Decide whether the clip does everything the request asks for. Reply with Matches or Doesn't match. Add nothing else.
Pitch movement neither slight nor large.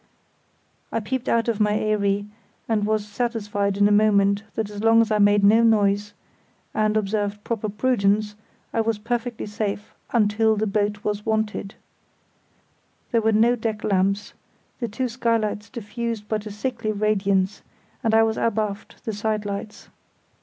Doesn't match